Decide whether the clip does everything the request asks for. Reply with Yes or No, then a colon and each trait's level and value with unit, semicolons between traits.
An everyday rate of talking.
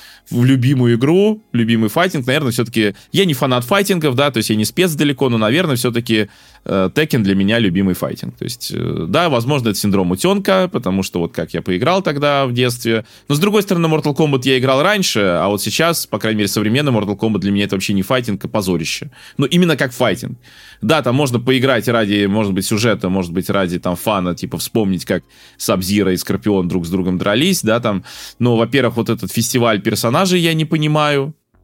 No: fast, 205 wpm